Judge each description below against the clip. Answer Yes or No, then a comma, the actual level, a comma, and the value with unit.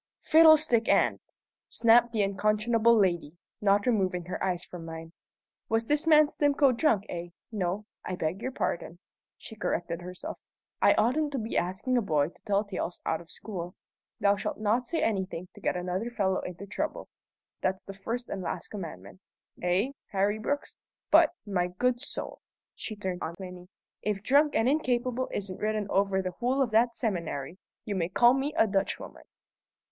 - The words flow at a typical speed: Yes, average, 170 wpm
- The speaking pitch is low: No, high, 205 Hz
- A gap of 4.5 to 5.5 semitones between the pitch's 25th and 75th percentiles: Yes, average, 4.8 semitones